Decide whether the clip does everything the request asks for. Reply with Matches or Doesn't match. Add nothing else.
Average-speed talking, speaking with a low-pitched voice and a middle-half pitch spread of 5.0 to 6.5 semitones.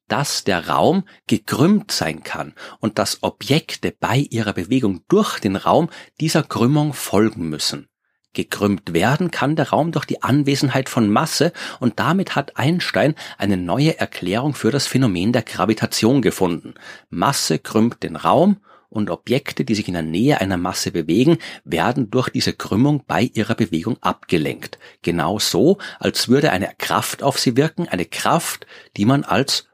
Matches